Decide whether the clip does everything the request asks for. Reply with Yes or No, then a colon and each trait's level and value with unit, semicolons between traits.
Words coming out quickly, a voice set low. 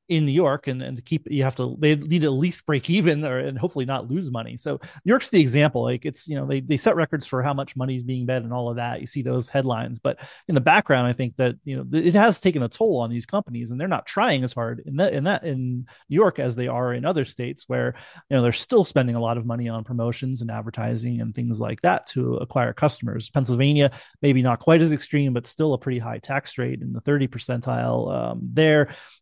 Yes: fast, 260 wpm; low, 130 Hz